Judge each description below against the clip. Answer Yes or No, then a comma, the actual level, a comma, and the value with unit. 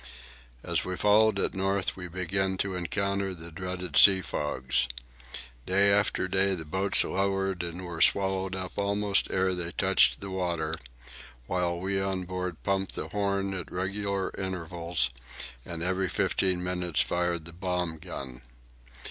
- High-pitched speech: No, very low, 95 Hz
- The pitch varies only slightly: Yes, narrow, 1.9 semitones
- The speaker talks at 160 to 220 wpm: No, average, 150 wpm